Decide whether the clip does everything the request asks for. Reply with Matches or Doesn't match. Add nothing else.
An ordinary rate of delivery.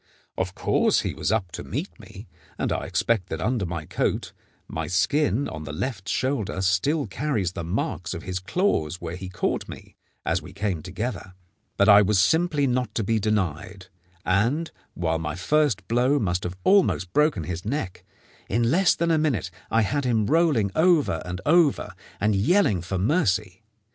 Matches